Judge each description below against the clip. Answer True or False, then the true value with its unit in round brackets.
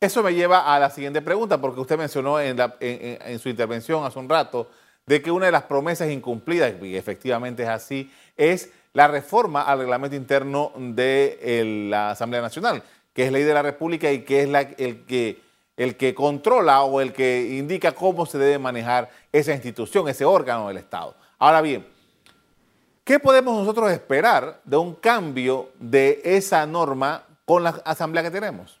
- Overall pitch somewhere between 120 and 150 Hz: True (140 Hz)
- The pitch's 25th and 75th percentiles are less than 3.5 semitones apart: False (4.0 semitones)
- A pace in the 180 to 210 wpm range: True (185 wpm)